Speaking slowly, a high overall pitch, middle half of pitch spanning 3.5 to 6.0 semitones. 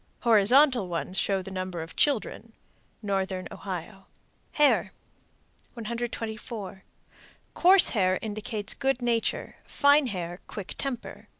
Yes: slow, 105 wpm; high, 215 Hz; average, 4.2 semitones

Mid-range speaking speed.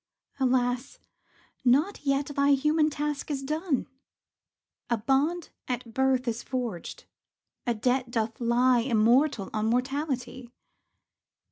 No: slow, 110 wpm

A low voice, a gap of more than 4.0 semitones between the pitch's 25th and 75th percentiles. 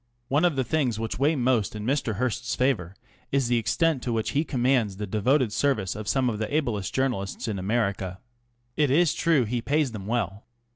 Yes: low, 120 Hz; average, 4.5 semitones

